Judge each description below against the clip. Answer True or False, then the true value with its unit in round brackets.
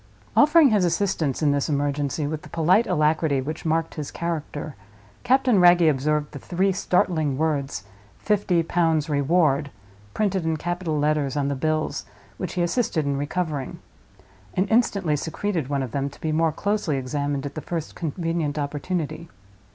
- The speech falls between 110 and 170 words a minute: True (160 wpm)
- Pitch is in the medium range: True (155 Hz)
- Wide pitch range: False (3.5 semitones)